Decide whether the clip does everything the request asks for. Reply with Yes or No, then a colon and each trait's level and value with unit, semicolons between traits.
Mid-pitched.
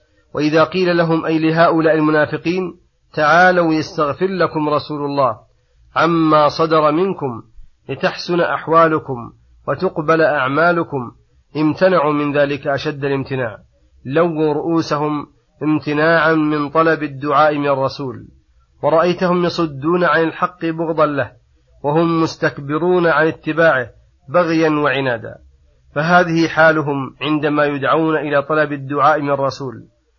Yes: medium, 155 Hz